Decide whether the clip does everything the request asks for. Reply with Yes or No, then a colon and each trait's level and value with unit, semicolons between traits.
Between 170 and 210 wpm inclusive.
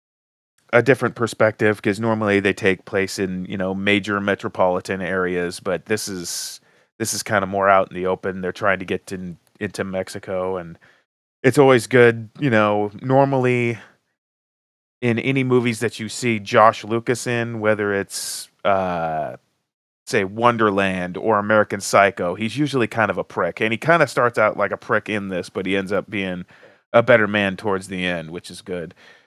Yes: average, 180 wpm